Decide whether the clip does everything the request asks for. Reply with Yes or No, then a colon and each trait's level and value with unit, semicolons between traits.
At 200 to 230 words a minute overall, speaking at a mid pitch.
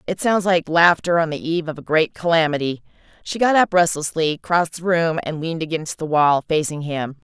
Yes: fast, 205 wpm; medium, 165 Hz